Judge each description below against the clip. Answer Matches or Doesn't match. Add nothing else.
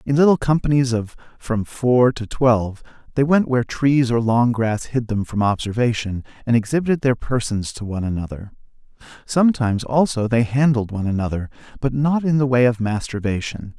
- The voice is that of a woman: Doesn't match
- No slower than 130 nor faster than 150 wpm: Doesn't match